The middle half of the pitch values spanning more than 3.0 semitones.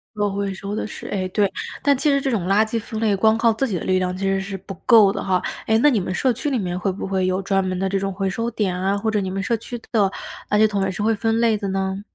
No: narrow, 2.6 semitones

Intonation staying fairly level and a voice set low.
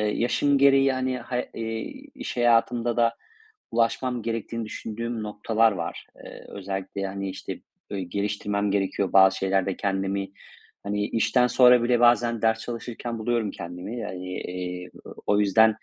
No: average, 3.4 semitones; low, 110 Hz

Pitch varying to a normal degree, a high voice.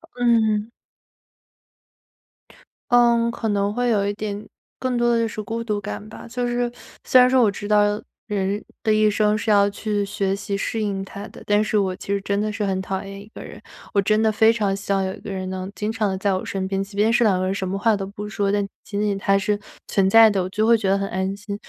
No: narrow, 1.9 semitones; high, 205 Hz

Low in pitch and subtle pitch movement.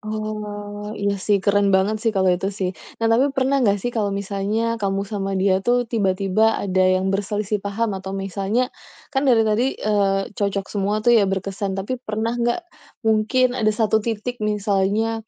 No: high, 205 Hz; narrow, 2.3 semitones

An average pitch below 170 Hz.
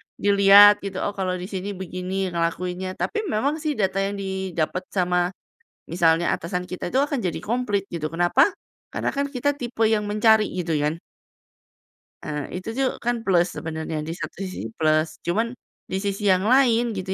No: high, 190 Hz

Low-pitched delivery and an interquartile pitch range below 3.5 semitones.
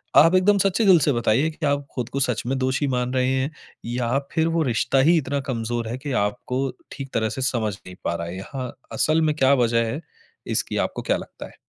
No: low, 130 Hz; average, 4.0 semitones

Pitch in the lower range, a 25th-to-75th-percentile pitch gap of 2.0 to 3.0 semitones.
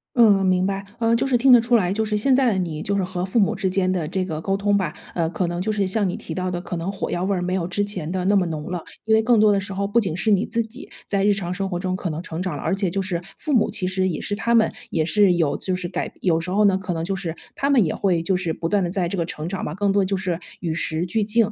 No: high, 190 Hz; average, 2.7 semitones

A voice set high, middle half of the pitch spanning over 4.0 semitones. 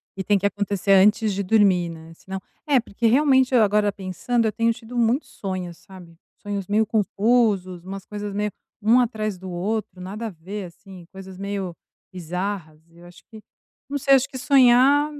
No: high, 205 Hz; average, 3.4 semitones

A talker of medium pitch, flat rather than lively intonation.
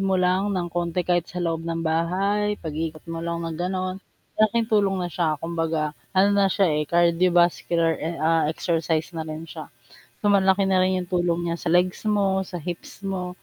Yes: medium, 175 Hz; narrow, 2.3 semitones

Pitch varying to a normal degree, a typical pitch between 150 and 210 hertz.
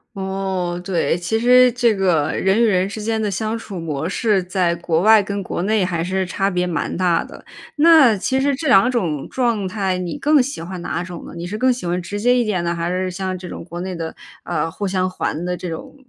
Yes: average, 3.8 semitones; high, 190 Hz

